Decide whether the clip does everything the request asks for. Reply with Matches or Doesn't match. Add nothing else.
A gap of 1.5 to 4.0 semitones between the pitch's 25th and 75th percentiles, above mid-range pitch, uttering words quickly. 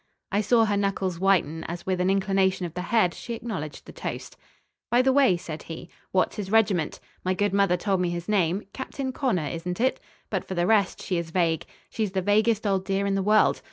Matches